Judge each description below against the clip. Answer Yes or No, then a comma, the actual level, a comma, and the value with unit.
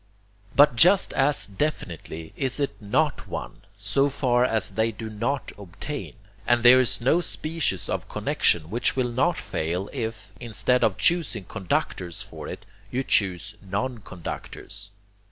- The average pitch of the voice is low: Yes, low, 115 Hz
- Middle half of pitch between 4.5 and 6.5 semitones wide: Yes, average, 5.1 semitones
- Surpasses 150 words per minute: No, average, 145 wpm